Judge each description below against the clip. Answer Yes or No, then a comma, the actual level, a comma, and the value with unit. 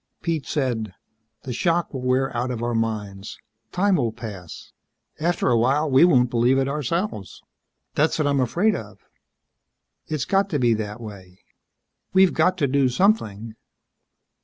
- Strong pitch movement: Yes, wide, 5.7 semitones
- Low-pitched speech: Yes, low, 130 Hz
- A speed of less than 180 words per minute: Yes, average, 155 wpm